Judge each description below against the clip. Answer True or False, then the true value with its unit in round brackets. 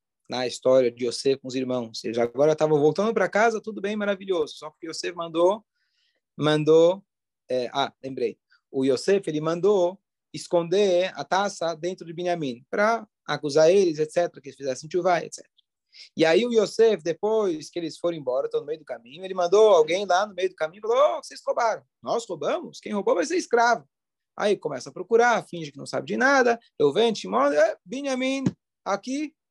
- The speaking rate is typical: False (190 wpm)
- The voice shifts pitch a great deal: True (6.9 semitones)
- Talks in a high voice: False (180 Hz)